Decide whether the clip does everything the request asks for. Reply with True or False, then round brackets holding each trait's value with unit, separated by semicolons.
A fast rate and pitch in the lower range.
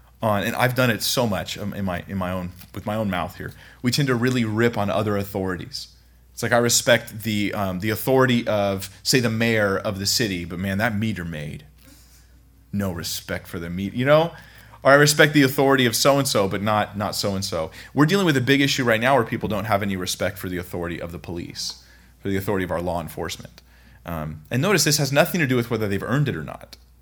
True (240 wpm; 105 Hz)